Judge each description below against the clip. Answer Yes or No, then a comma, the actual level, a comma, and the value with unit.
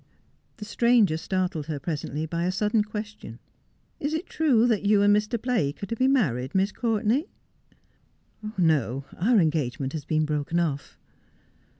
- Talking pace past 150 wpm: Yes, average, 175 wpm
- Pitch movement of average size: No, wide, 6.1 semitones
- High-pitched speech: Yes, high, 195 Hz